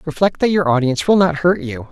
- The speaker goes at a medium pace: No, fast, 250 wpm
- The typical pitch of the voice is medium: Yes, medium, 155 Hz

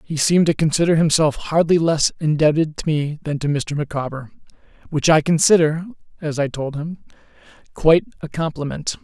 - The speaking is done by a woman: No, male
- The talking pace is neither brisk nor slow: Yes, average, 160 wpm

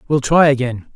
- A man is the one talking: Yes, male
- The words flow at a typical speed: Yes, average, 190 wpm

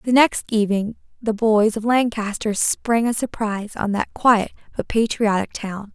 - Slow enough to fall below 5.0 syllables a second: Yes, 4.5 syllables/s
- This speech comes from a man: No, female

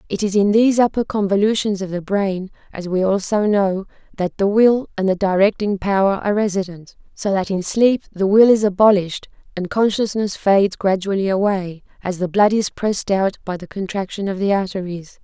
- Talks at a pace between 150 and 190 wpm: Yes, average, 185 wpm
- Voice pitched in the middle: No, high, 195 Hz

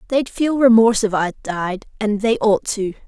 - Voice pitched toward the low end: No, high, 220 Hz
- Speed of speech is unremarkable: Yes, average, 195 wpm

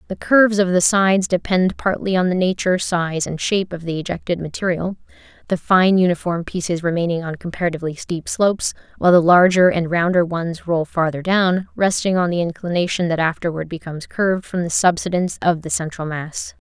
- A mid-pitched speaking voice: Yes, medium, 175 Hz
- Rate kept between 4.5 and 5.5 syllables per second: No, 5.7 syllables/s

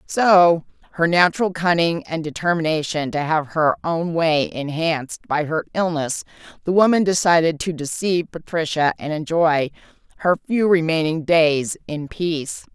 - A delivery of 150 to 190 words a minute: No, slow, 135 wpm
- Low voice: No, medium, 165 Hz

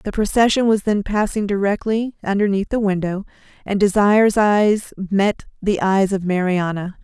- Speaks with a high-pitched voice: Yes, high, 200 Hz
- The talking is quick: No, average, 145 wpm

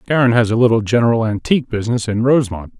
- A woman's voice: No, male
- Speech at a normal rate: Yes, average, 195 wpm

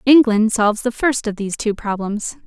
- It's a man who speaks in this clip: No, female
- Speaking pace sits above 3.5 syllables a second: Yes, 5.3 syllables/s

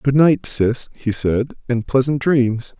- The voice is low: Yes, low, 125 Hz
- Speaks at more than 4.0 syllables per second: No, 3.6 syllables/s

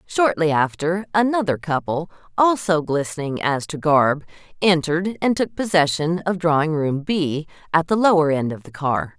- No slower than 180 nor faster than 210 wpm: No, average, 155 wpm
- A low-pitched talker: No, medium, 165 Hz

